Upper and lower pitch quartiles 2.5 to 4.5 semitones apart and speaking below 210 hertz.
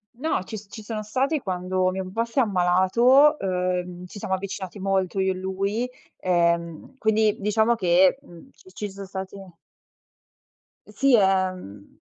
Yes: average, 2.9 semitones; high, 190 Hz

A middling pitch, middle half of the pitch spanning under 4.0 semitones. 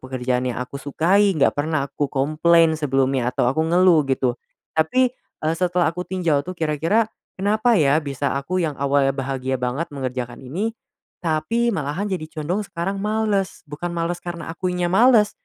No: medium, 160 Hz; average, 5.0 semitones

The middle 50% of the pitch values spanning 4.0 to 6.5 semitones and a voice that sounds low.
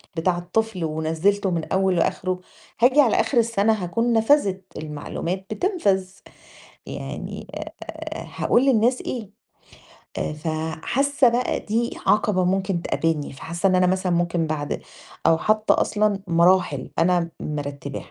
No: average, 4.8 semitones; high, 190 Hz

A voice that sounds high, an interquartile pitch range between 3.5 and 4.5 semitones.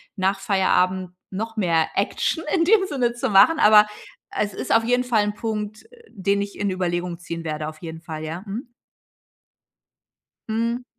Yes: high, 200 Hz; average, 4.1 semitones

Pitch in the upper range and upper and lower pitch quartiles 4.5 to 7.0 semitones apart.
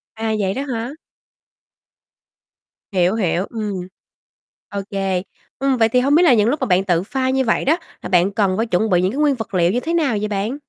Yes: high, 220 Hz; average, 5.3 semitones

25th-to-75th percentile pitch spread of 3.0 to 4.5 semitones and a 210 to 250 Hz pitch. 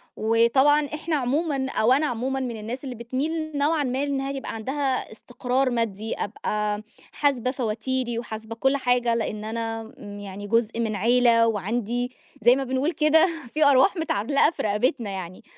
Yes: average, 3.5 semitones; high, 245 Hz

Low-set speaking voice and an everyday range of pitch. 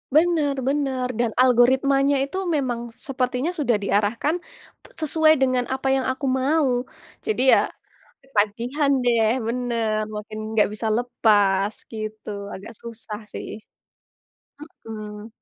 No: high, 245 Hz; average, 4.1 semitones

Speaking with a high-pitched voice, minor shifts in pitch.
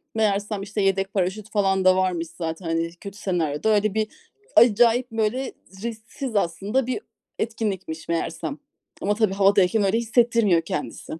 No: high, 200 Hz; average, 3.3 semitones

